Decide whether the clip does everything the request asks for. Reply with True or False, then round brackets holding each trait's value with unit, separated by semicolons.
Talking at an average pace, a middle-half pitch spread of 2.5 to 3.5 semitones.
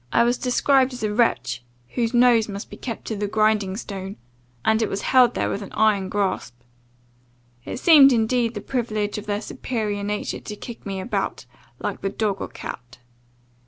True (185 wpm; 3.1 semitones)